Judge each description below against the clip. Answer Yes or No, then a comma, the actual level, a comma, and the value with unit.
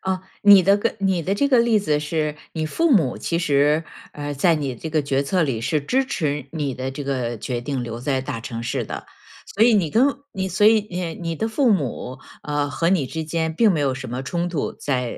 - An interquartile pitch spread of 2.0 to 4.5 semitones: No, wide, 5.6 semitones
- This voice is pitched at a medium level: Yes, medium, 155 Hz